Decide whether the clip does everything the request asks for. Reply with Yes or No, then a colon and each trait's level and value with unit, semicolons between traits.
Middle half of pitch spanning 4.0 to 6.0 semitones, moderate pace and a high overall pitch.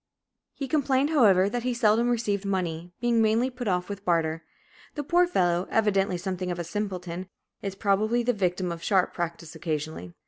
Yes: average, 5.1 semitones; average, 175 wpm; high, 195 Hz